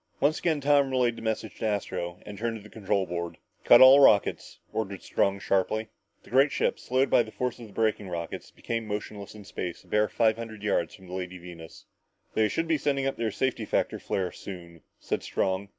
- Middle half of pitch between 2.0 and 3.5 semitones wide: No, average, 4.2 semitones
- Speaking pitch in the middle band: No, low, 105 Hz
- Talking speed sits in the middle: No, fast, 215 wpm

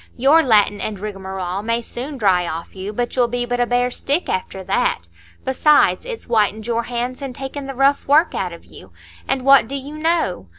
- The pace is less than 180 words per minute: No, fast, 205 wpm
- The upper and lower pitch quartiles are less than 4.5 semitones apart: No, average, 5.3 semitones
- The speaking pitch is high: Yes, high, 245 Hz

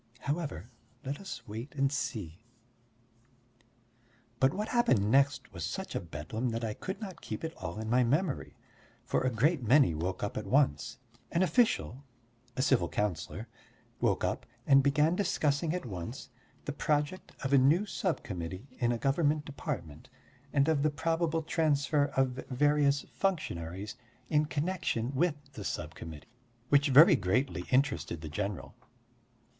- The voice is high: No, low, 135 Hz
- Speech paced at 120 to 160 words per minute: Yes, average, 150 wpm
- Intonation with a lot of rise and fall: Yes, wide, 5.9 semitones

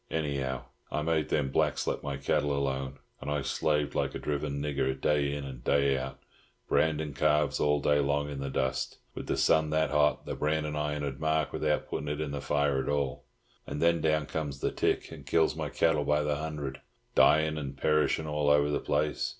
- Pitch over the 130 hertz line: No, very low, 75 Hz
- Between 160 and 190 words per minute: No, fast, 205 wpm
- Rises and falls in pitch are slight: Yes, narrow, 1.5 semitones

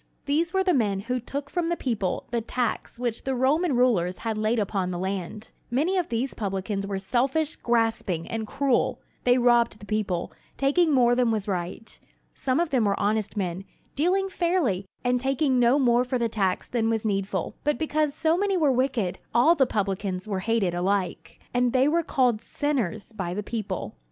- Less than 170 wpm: No, average, 190 wpm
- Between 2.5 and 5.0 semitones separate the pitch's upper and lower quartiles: No, wide, 5.4 semitones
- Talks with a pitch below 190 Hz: No, high, 235 Hz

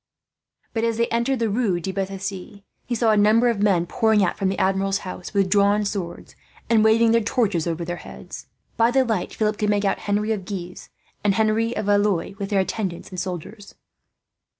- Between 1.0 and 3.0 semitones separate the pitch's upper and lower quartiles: Yes, narrow, 2.5 semitones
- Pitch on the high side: Yes, high, 205 Hz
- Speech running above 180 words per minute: Yes, average, 200 wpm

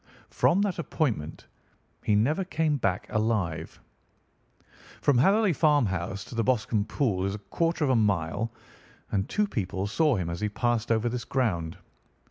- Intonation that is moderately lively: No, wide, 7.0 semitones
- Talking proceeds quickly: No, average, 155 wpm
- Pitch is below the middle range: Yes, low, 115 Hz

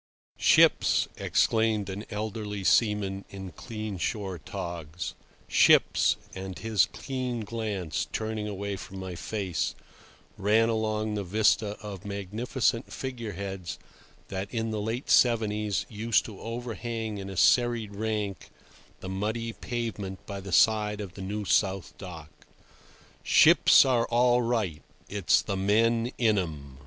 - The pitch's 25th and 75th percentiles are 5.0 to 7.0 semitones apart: No, average, 2.7 semitones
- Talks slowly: Yes, slow, 125 wpm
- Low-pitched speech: Yes, low, 105 Hz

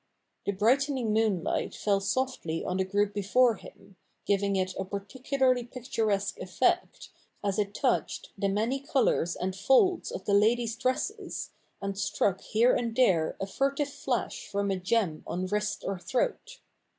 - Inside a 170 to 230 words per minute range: No, average, 160 wpm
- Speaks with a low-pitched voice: No, high, 210 Hz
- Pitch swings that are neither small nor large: Yes, average, 4.5 semitones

